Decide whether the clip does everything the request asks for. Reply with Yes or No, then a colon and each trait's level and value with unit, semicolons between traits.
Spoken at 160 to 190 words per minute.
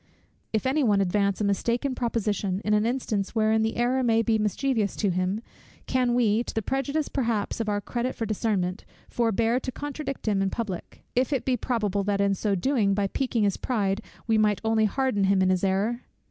No: average, 200 wpm